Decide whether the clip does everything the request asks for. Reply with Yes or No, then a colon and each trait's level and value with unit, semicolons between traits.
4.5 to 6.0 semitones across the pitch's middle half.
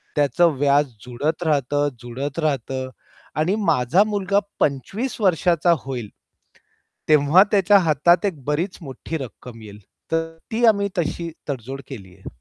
Yes: average, 5.0 semitones